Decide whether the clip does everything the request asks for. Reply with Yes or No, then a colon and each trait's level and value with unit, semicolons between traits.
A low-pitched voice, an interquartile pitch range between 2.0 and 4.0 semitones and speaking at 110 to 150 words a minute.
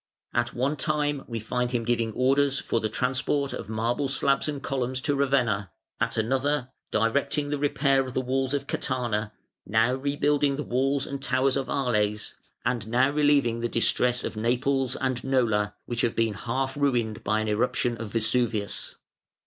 No: low, 130 Hz; average, 3.3 semitones; average, 170 wpm